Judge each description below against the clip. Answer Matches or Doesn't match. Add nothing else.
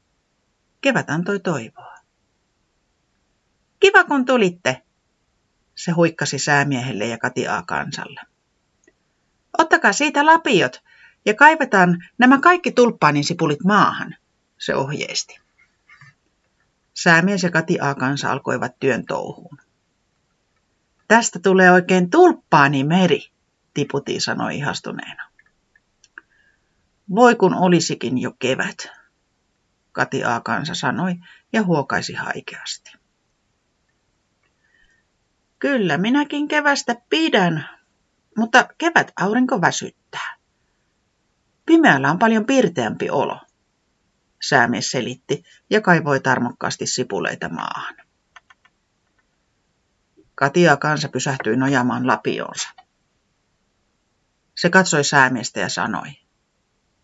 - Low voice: Doesn't match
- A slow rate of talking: Matches